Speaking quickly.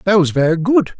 Yes: fast, 240 wpm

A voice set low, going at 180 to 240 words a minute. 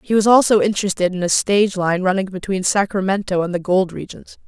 No: high, 190 Hz; average, 200 wpm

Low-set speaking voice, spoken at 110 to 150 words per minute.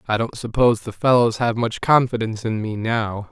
No: low, 115 Hz; average, 200 wpm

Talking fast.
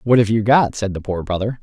Yes: fast, 295 wpm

